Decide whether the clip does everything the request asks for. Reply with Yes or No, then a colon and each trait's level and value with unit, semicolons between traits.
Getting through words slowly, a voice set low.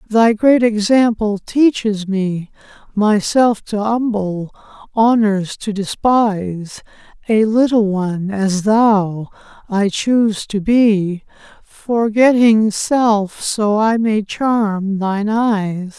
No: slow, 100 wpm; high, 210 Hz